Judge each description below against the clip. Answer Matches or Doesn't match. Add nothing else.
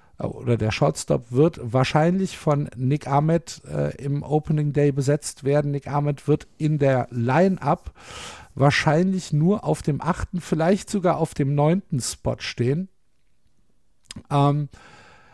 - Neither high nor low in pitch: Matches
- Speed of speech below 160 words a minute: Matches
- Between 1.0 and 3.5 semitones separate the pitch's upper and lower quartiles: Matches